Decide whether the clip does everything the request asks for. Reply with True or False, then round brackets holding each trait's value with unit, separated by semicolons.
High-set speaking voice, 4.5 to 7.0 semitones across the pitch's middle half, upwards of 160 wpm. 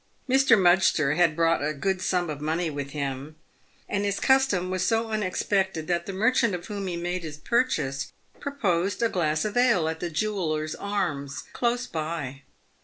False (180 Hz; 4.9 semitones; 175 wpm)